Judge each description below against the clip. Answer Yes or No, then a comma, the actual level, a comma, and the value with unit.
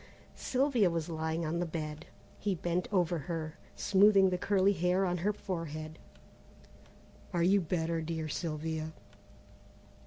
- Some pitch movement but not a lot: Yes, average, 3.0 semitones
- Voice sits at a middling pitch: Yes, medium, 170 Hz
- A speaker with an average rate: No, slow, 130 wpm